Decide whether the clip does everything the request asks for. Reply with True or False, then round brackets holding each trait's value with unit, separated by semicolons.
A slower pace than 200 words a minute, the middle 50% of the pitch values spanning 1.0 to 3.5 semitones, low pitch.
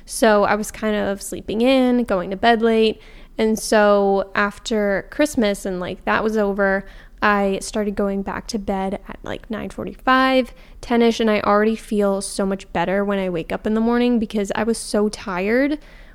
False (190 wpm; 2.5 semitones; 210 Hz)